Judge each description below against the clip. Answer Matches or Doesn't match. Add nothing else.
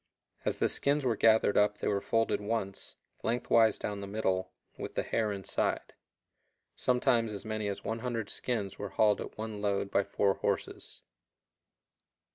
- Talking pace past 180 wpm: Doesn't match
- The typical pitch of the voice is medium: Doesn't match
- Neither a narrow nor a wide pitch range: Doesn't match